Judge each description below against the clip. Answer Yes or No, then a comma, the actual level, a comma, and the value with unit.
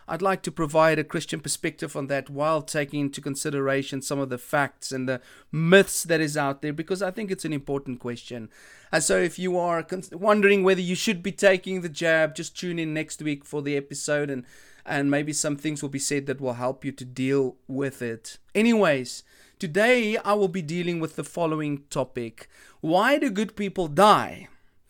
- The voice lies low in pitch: No, medium, 155 Hz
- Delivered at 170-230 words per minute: Yes, average, 200 wpm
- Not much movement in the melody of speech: No, average, 4.8 semitones